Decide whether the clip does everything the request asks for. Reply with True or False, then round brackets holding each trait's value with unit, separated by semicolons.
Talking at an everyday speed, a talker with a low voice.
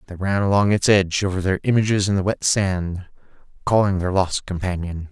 True (190 wpm; 95 Hz)